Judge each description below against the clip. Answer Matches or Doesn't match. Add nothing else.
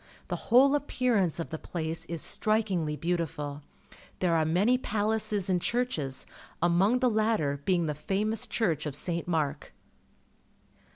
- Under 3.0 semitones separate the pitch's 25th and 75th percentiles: Doesn't match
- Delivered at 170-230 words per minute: Doesn't match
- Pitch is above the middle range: Doesn't match